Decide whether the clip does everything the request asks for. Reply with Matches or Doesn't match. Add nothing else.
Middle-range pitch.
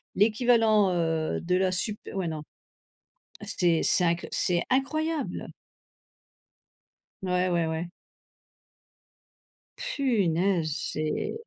Matches